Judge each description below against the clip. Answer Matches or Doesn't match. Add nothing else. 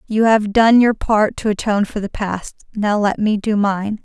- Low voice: Doesn't match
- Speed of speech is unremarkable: Doesn't match